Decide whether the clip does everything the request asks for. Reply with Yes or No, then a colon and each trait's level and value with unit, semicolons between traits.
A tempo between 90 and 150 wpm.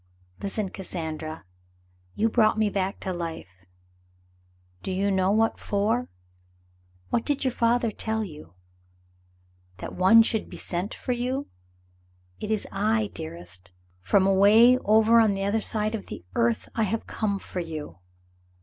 Yes: average, 145 wpm